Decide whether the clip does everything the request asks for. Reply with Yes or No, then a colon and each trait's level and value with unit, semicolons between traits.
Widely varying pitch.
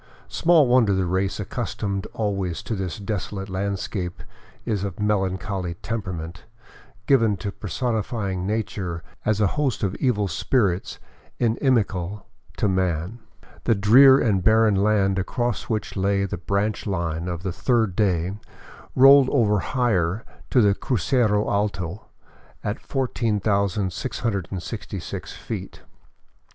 No: average, 3.2 semitones